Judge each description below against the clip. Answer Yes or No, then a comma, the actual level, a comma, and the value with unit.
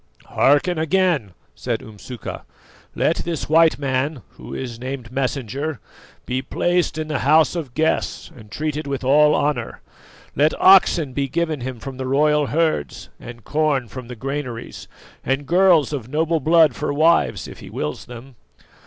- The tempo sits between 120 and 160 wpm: Yes, average, 155 wpm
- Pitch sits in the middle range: Yes, medium, 145 Hz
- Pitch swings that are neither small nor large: Yes, average, 3.6 semitones